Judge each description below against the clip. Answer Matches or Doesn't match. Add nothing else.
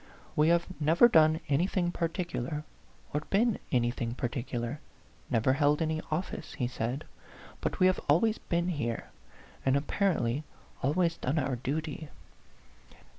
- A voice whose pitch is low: Doesn't match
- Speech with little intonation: Doesn't match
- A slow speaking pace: Matches